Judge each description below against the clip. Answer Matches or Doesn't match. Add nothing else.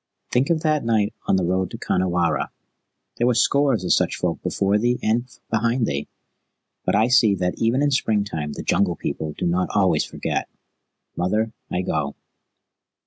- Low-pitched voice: Matches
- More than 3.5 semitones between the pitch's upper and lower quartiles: Matches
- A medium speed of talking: Matches